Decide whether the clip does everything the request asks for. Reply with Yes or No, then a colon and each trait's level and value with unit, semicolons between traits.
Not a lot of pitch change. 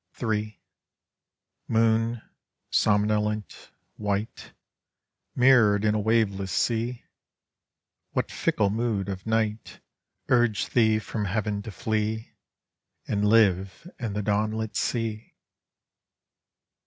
Yes: narrow, 1.6 semitones